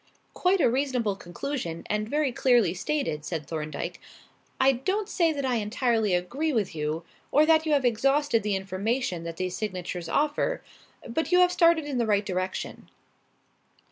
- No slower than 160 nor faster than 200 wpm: Yes, average, 165 wpm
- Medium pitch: No, high, 235 Hz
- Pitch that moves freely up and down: Yes, wide, 7.8 semitones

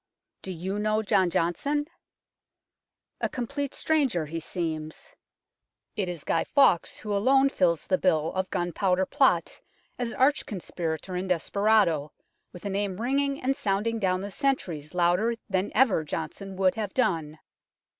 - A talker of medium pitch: No, high, 195 Hz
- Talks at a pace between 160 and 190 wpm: No, average, 145 wpm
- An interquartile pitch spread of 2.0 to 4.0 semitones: No, average, 4.8 semitones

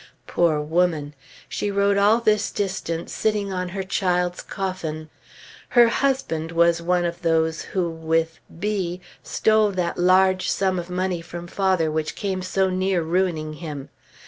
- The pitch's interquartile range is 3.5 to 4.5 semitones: No, average, 2.8 semitones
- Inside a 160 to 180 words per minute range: No, average, 145 wpm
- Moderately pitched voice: Yes, medium, 180 Hz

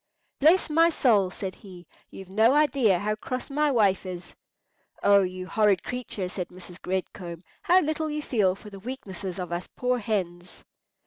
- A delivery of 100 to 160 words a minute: No, average, 175 wpm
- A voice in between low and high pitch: No, high, 200 Hz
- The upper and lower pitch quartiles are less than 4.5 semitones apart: No, wide, 5.6 semitones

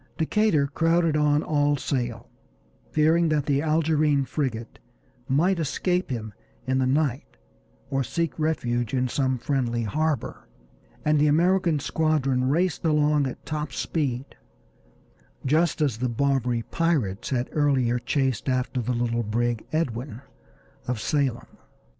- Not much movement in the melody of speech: No, average, 3.8 semitones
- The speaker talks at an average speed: No, slow, 130 wpm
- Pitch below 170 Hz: Yes, medium, 140 Hz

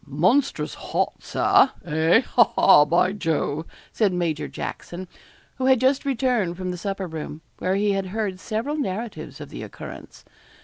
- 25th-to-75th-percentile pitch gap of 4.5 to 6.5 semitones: Yes, wide, 5.5 semitones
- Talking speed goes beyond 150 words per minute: Yes, average, 160 wpm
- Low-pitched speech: No, high, 190 Hz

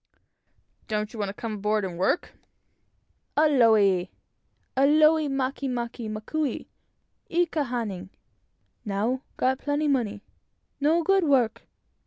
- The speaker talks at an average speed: No, slow, 115 wpm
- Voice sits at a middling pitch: No, high, 245 Hz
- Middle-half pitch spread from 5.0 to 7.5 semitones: Yes, wide, 5.6 semitones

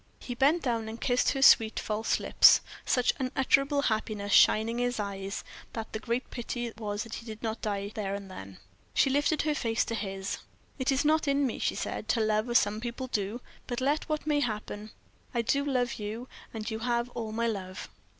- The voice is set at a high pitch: Yes, high, 230 Hz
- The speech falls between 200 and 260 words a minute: Yes, fast, 205 wpm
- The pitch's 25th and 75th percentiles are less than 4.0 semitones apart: Yes, average, 3.2 semitones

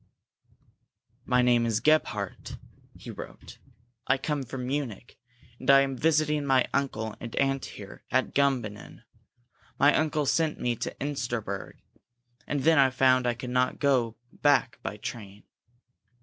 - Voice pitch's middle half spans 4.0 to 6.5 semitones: No, average, 3.1 semitones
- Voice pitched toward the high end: No, low, 130 Hz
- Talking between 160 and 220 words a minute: No, average, 140 wpm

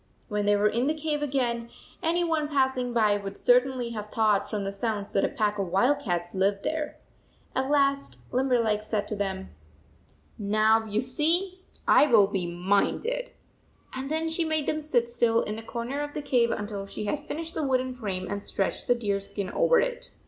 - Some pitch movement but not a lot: No, wide, 6.0 semitones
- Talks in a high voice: Yes, high, 235 Hz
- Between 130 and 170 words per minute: No, average, 195 wpm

